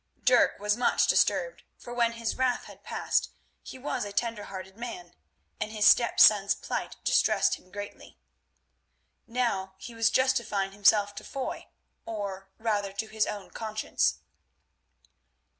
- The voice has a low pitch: No, high, 215 Hz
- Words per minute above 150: No, average, 140 wpm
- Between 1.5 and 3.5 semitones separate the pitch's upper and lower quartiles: Yes, average, 2.8 semitones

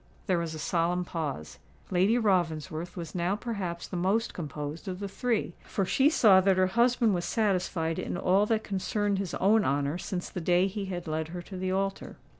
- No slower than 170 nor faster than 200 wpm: Yes, average, 195 wpm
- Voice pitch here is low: No, medium, 185 Hz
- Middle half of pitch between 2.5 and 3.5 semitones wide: Yes, average, 2.9 semitones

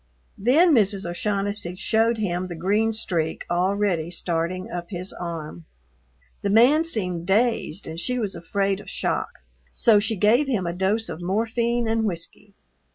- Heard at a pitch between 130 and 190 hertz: No, high, 200 Hz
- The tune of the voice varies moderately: Yes, average, 4.2 semitones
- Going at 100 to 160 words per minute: Yes, average, 155 wpm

